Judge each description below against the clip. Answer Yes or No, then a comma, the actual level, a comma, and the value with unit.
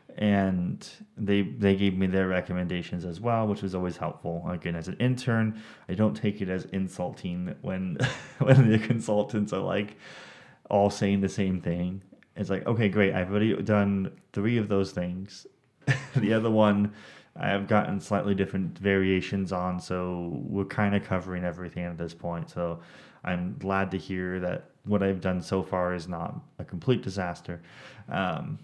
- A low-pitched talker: Yes, low, 100 Hz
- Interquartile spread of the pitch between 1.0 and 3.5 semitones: Yes, average, 2.9 semitones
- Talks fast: No, average, 170 wpm